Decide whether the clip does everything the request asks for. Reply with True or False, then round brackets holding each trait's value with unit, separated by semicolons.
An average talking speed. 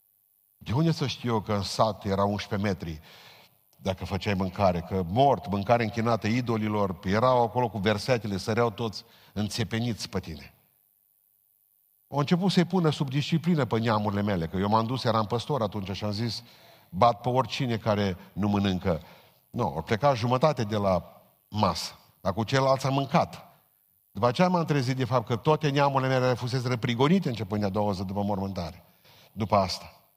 False (175 wpm)